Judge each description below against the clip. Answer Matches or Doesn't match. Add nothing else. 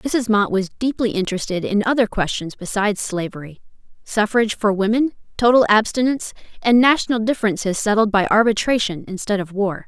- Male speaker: Doesn't match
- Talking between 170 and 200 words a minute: Doesn't match